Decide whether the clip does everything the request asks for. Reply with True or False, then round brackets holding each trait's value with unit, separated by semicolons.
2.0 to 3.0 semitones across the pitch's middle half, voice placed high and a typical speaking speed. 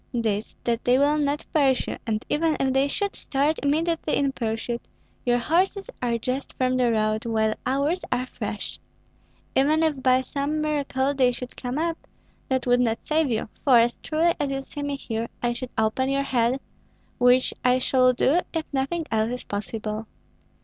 False (3.5 semitones; 260 Hz; 180 wpm)